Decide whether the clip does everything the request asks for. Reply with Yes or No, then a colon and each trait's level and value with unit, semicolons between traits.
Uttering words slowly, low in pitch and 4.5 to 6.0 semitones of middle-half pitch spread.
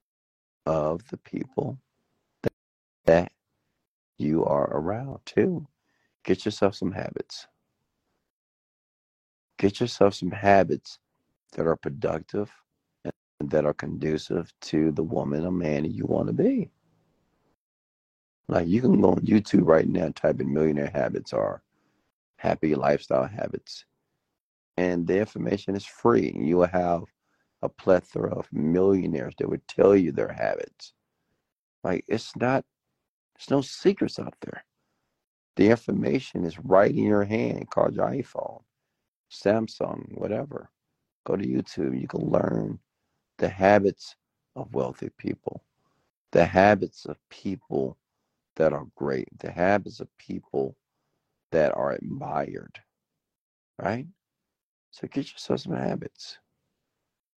Yes: slow, 125 wpm; very low, 90 Hz; average, 5.3 semitones